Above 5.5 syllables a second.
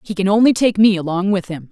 Yes: 6.2 syllables/s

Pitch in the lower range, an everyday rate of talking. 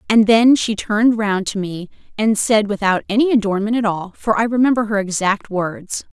No: high, 210 Hz; average, 195 wpm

